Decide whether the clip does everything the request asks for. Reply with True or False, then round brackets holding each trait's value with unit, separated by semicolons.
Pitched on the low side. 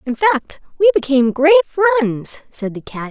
False (295 Hz)